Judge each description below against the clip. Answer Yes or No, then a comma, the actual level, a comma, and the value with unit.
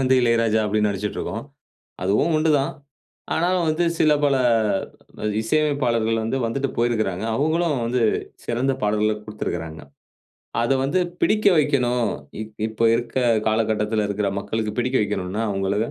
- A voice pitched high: No, low, 115 Hz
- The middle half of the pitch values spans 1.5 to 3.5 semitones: No, average, 4.4 semitones